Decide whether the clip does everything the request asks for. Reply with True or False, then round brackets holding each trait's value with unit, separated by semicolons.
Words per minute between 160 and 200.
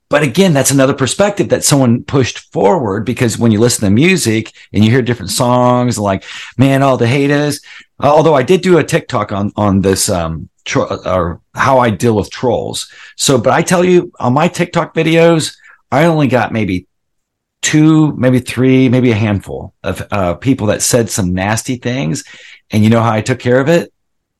True (190 wpm)